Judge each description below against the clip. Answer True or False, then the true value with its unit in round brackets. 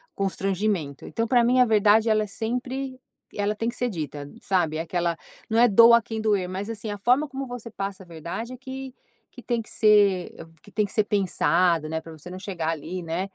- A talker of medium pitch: False (205 Hz)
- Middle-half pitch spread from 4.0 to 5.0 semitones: True (4.7 semitones)